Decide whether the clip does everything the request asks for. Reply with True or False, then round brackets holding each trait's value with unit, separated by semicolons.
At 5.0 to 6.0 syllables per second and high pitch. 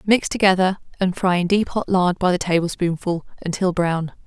False (5.1 syllables/s; 180 Hz)